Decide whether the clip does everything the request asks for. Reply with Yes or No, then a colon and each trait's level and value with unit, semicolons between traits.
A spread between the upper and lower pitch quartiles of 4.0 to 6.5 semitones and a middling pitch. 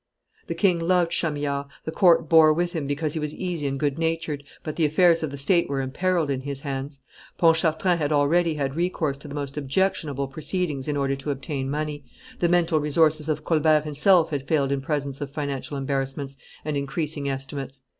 No: average, 2.8 semitones; medium, 150 Hz